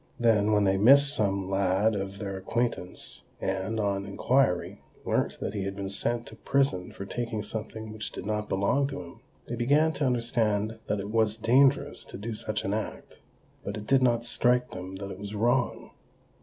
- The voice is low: Yes, low, 110 Hz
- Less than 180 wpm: No, average, 185 wpm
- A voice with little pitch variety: No, average, 3.4 semitones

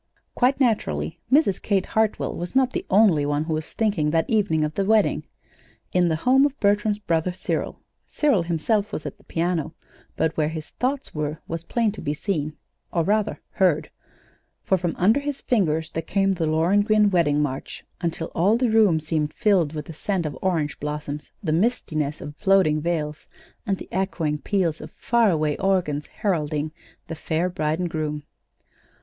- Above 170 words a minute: Yes, average, 180 wpm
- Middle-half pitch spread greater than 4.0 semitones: Yes, average, 5.0 semitones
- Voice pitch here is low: No, medium, 170 Hz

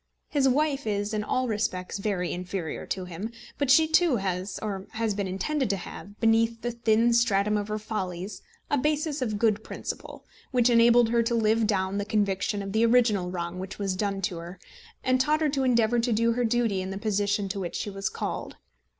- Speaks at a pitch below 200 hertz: No, high, 215 Hz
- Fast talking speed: Yes, fast, 210 wpm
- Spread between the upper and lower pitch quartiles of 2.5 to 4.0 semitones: Yes, average, 3.5 semitones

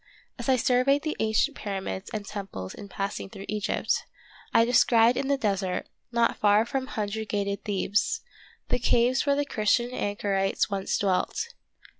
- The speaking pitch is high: Yes, high, 215 Hz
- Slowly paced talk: No, average, 155 wpm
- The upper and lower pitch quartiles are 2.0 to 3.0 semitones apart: No, average, 3.9 semitones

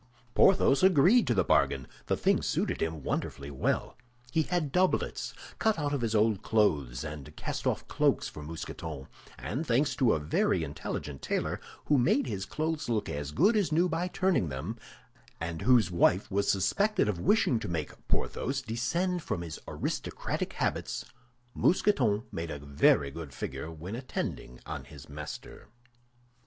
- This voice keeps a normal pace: Yes, average, 160 wpm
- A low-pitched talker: Yes, low, 105 Hz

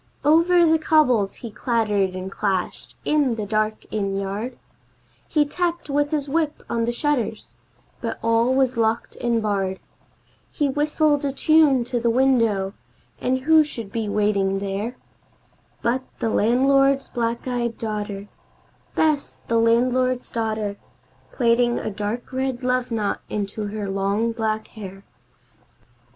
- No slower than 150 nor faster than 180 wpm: No, average, 140 wpm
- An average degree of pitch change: Yes, average, 4.2 semitones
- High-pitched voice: Yes, high, 235 Hz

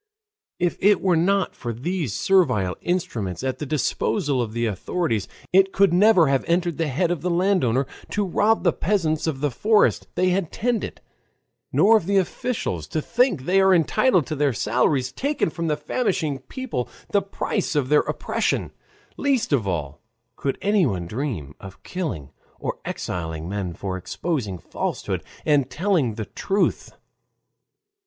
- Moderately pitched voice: Yes, medium, 155 Hz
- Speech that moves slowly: No, average, 160 wpm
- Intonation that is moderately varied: No, wide, 8.3 semitones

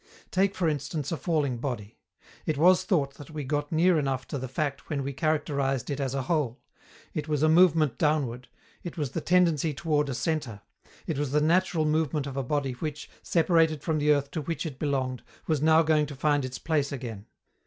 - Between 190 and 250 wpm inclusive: Yes, fast, 205 wpm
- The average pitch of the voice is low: No, medium, 150 Hz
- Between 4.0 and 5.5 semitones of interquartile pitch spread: No, narrow, 2.6 semitones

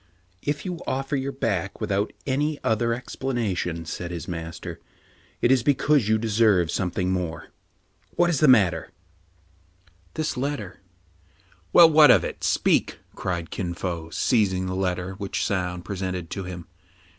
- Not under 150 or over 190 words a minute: Yes, average, 170 wpm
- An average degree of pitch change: No, wide, 6.1 semitones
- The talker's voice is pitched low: Yes, very low, 95 Hz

